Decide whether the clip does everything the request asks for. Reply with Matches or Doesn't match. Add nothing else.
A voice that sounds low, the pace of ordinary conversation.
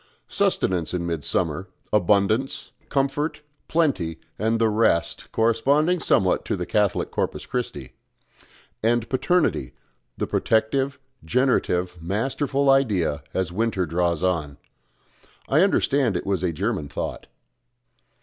Doesn't match